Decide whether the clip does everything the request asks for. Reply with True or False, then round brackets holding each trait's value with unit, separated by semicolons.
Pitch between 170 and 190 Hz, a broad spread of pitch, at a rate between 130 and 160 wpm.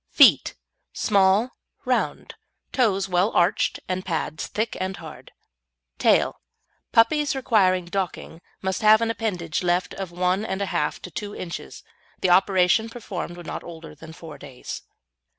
False (185 Hz; 3.2 semitones; 150 wpm)